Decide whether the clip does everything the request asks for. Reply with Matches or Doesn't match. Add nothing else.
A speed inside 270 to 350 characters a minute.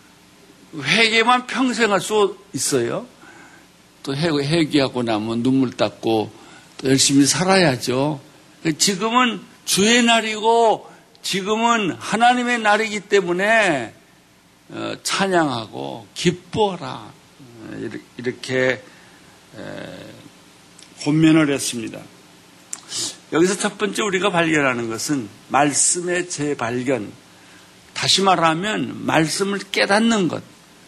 Doesn't match